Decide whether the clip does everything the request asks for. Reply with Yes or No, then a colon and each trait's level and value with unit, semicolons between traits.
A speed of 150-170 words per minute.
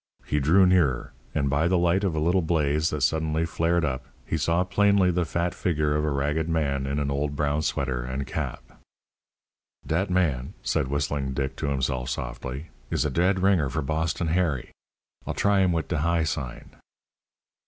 No: average, 185 wpm